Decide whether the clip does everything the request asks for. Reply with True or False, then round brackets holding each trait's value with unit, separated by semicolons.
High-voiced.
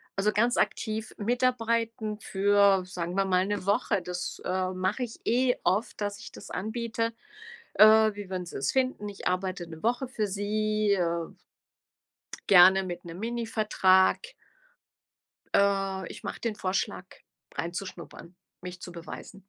True (200 Hz)